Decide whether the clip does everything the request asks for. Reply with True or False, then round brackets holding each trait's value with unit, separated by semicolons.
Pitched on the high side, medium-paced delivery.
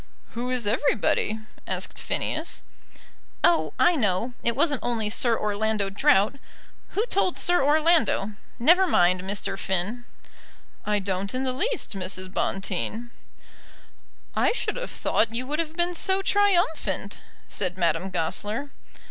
False (235 Hz; 130 wpm)